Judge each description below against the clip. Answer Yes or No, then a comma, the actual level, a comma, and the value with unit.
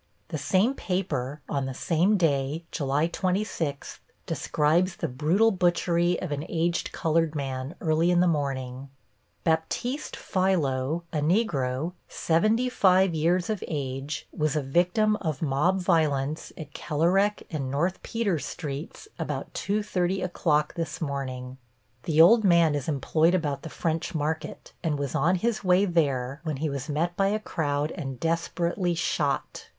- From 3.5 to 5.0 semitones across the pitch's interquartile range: Yes, average, 4.1 semitones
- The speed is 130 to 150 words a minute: Yes, average, 145 wpm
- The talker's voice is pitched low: No, medium, 160 Hz